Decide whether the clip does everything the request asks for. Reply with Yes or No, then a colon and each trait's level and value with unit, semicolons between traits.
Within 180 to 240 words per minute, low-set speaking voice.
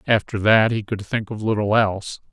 Yes: fast, 205 wpm; low, 105 Hz